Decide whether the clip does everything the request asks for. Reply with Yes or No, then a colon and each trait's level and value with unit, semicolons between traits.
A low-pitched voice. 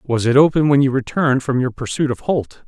Yes: low, 130 Hz